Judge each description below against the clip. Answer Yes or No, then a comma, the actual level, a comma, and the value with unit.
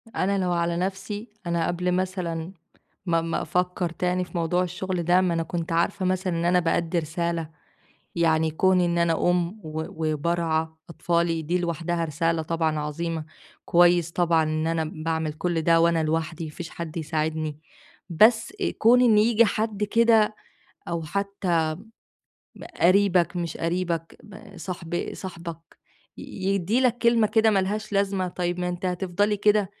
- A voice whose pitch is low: No, medium, 175 Hz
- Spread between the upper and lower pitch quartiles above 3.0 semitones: No, narrow, 2.4 semitones